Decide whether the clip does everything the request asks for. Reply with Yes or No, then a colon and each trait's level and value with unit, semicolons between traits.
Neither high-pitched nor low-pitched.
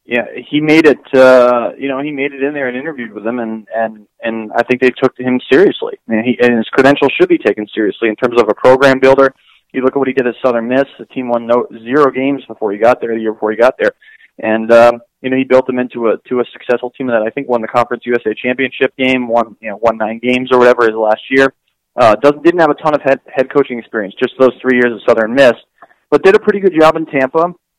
No: low, 125 Hz